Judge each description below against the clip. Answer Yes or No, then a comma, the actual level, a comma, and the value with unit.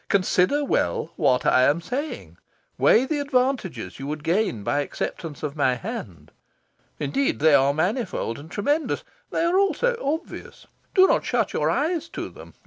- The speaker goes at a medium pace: Yes, average, 160 wpm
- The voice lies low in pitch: No, medium, 185 Hz